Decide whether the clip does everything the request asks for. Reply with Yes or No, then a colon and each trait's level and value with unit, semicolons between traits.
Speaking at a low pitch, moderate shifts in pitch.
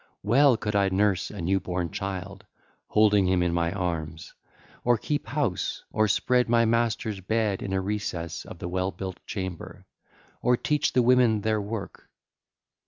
Yes: low, 100 Hz; average, 3.5 semitones